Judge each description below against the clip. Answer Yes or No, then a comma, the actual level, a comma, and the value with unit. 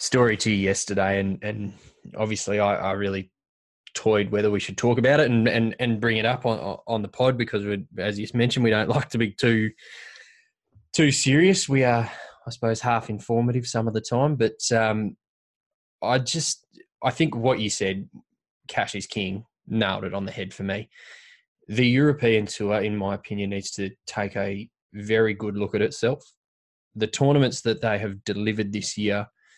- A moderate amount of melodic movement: Yes, average, 3.1 semitones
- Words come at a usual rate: Yes, average, 185 wpm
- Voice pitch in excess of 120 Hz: No, low, 110 Hz